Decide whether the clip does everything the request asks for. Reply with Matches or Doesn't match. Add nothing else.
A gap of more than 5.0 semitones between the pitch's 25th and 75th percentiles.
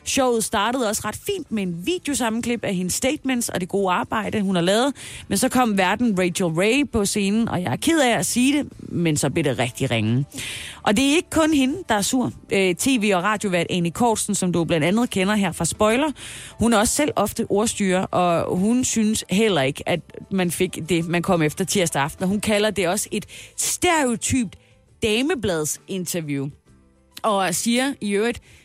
Matches